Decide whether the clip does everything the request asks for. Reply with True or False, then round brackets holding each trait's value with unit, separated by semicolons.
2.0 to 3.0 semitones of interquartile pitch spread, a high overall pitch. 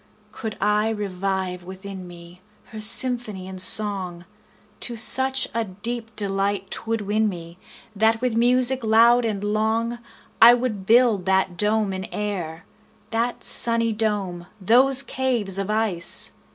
False (3.4 semitones; 215 Hz)